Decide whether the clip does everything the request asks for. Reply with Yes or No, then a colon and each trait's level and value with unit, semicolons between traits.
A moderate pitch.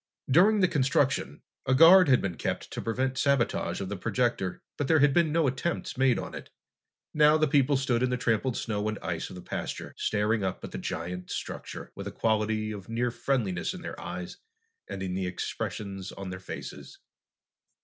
No: low, 120 Hz